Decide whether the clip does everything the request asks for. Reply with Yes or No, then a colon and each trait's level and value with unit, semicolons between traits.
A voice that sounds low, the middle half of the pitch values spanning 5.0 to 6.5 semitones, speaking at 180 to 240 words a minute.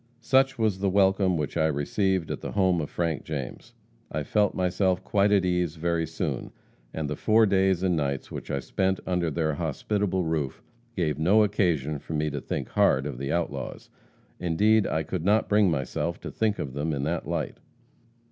No: very low, 85 Hz; average, 4.2 semitones; average, 190 wpm